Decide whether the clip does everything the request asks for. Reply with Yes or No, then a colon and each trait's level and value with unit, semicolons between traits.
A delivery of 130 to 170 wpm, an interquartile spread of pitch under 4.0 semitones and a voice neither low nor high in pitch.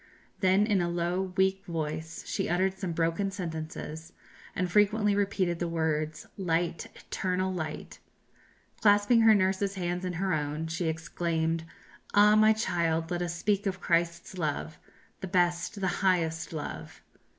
Yes: average, 145 wpm; average, 2.8 semitones; medium, 175 Hz